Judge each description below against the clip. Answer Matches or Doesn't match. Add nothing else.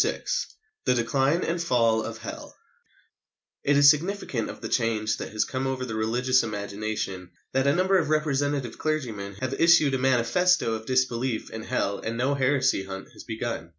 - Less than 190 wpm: Matches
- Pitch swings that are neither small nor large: Matches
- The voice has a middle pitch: Doesn't match